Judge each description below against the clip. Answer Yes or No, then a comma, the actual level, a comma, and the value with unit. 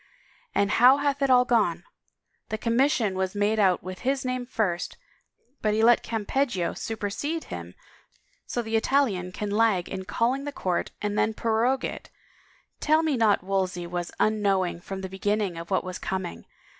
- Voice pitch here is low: No, high, 210 Hz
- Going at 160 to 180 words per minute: Yes, average, 170 wpm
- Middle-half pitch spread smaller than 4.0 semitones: No, average, 4.7 semitones